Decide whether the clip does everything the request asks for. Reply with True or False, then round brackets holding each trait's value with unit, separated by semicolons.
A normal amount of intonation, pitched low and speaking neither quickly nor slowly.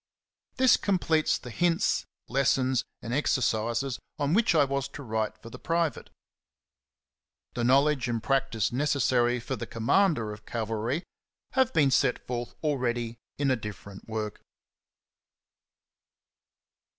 False (4.1 semitones; 130 Hz; 130 wpm)